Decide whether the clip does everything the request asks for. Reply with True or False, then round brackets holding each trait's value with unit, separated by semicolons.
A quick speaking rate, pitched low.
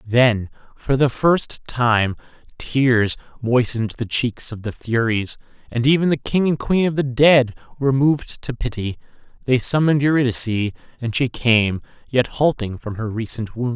False (160 wpm; 125 Hz)